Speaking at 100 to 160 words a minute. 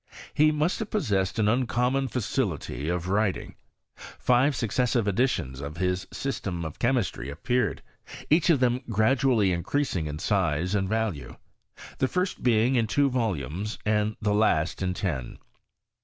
Yes: average, 140 wpm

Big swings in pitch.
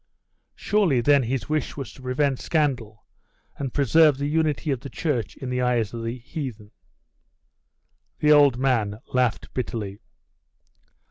No: average, 3.7 semitones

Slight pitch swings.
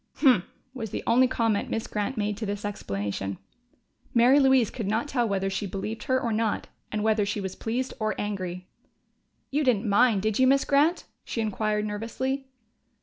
No: average, 3.7 semitones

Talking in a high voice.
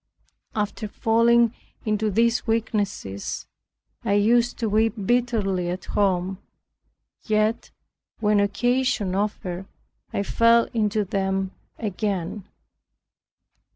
Yes: high, 210 Hz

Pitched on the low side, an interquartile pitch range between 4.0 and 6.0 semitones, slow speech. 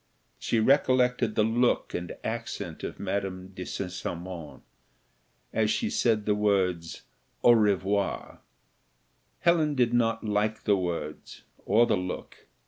Yes: low, 105 Hz; average, 4.3 semitones; slow, 130 wpm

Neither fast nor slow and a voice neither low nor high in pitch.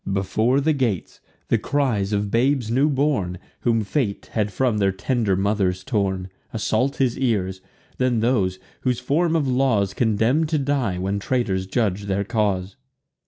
No: average, 155 wpm; low, 110 Hz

